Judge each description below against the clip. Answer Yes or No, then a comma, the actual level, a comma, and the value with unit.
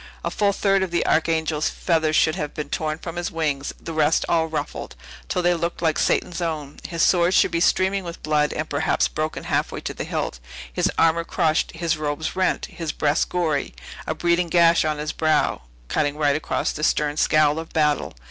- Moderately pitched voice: Yes, medium, 160 Hz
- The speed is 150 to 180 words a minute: No, average, 200 wpm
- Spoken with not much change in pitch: Yes, narrow, 1.9 semitones